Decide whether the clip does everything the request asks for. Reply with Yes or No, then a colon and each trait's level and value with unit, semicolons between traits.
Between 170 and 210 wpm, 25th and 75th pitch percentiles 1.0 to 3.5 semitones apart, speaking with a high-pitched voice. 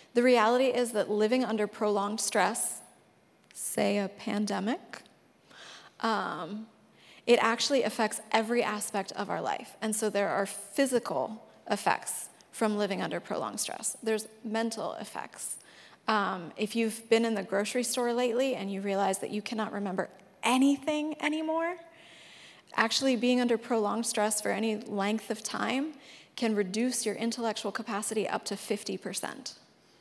No: average, 140 wpm; average, 2.8 semitones; high, 220 Hz